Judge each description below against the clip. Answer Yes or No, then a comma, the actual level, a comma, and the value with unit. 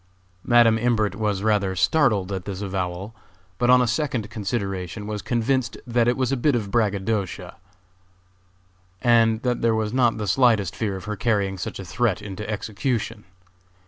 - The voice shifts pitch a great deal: No, average, 3.4 semitones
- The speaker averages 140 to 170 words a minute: Yes, average, 165 wpm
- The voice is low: Yes, low, 110 Hz